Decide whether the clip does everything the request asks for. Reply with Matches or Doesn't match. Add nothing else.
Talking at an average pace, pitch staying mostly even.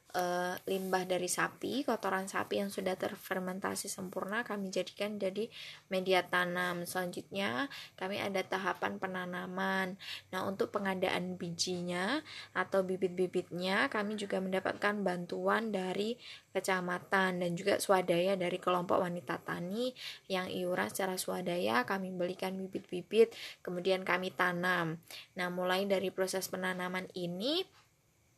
Matches